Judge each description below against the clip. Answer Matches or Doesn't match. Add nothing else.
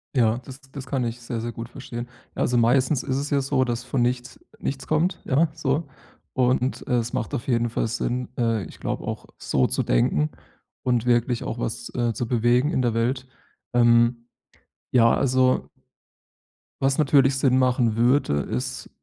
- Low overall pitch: Matches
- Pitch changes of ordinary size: Doesn't match